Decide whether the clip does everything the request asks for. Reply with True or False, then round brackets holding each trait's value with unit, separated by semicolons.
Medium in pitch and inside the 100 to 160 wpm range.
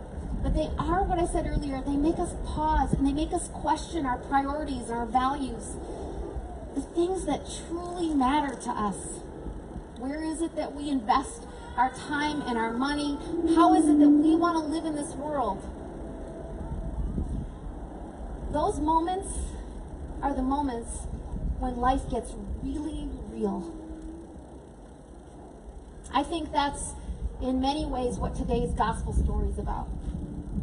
False (275 Hz; 140 wpm)